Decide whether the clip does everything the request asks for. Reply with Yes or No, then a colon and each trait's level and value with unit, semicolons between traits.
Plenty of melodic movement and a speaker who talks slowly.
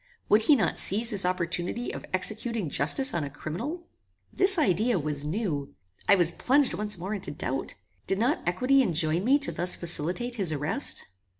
No: wide, 6.2 semitones; average, 175 wpm